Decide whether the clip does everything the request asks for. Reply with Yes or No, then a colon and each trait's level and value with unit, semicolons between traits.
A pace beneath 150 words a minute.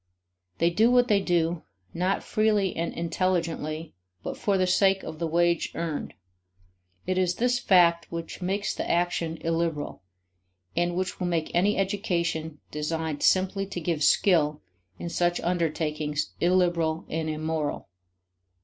Yes: average, 140 wpm